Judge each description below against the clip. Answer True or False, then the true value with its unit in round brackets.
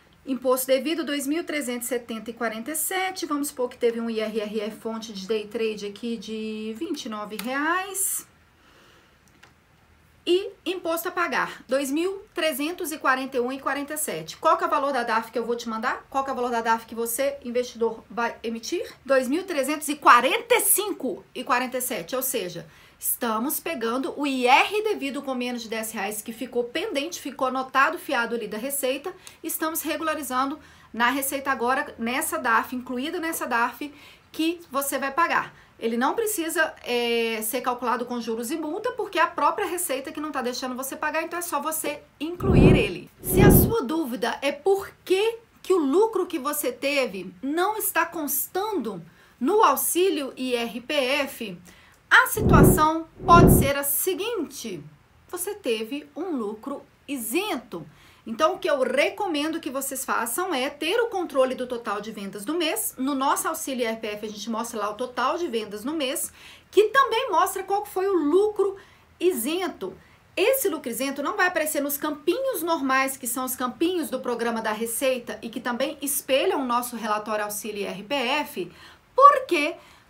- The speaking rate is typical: True (155 wpm)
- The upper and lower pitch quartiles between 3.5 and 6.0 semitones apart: True (5.4 semitones)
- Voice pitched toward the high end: True (275 Hz)